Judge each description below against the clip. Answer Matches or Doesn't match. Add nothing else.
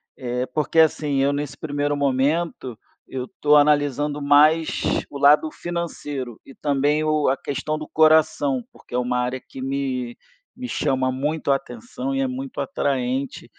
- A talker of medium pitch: Matches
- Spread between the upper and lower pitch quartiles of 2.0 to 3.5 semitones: Matches